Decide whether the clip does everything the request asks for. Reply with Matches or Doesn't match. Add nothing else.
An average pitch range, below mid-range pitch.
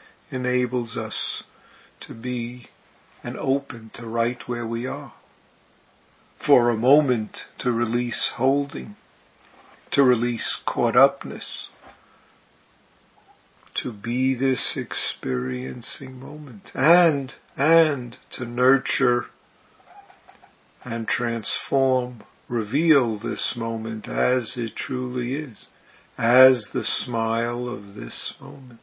Doesn't match